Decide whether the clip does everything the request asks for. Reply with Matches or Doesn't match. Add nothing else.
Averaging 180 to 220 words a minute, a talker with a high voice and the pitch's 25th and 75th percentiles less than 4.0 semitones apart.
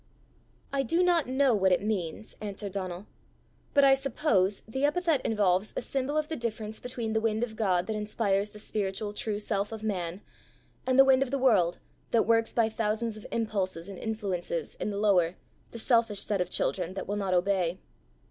Matches